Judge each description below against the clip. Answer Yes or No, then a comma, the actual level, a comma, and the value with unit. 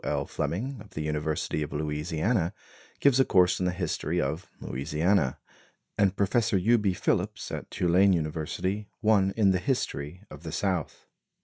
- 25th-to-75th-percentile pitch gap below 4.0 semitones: No, average, 4.7 semitones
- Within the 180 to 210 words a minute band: No, average, 155 wpm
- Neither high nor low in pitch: No, very low, 90 Hz